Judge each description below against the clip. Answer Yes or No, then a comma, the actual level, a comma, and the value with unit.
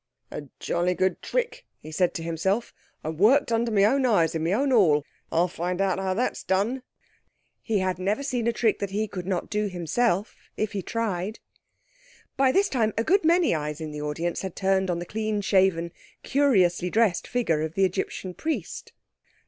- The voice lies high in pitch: Yes, high, 195 Hz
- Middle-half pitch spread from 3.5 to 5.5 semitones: Yes, average, 4.8 semitones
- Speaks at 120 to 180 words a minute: No, average, 190 wpm